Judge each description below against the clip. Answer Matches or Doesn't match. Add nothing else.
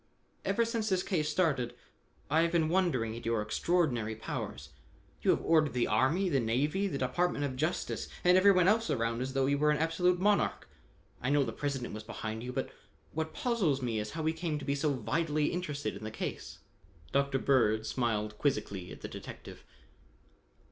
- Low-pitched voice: Doesn't match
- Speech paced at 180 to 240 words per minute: Matches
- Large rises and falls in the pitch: Matches